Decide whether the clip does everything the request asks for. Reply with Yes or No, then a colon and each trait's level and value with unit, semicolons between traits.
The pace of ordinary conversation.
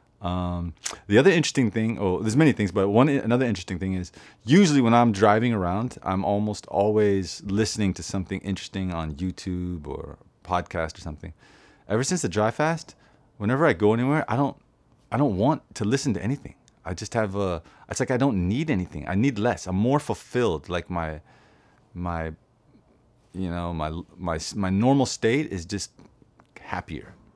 Yes: average, 175 wpm